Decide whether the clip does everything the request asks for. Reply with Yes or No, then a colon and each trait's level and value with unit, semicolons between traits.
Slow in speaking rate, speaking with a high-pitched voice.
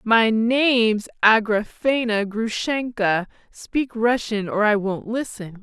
Yes: slow, 105 wpm; high, 220 Hz